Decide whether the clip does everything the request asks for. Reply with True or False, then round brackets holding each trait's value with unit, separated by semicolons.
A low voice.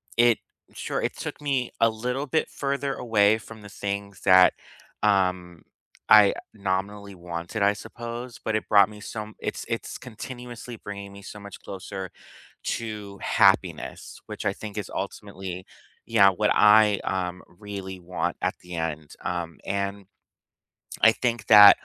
True (100 Hz)